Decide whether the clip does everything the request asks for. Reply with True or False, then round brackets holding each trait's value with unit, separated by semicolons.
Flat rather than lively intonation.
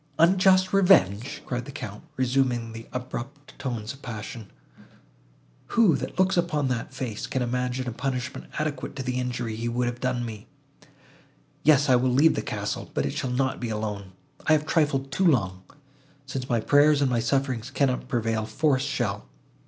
False (3.2 semitones)